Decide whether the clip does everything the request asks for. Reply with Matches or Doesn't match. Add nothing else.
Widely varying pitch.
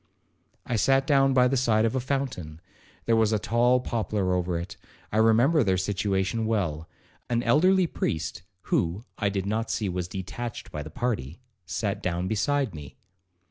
Doesn't match